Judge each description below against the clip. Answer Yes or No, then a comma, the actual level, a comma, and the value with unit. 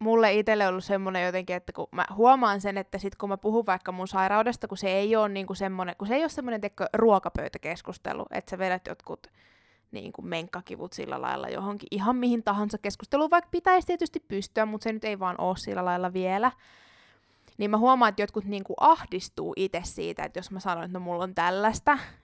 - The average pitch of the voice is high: Yes, high, 205 Hz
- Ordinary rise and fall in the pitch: Yes, average, 3.4 semitones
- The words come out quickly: Yes, fast, 205 wpm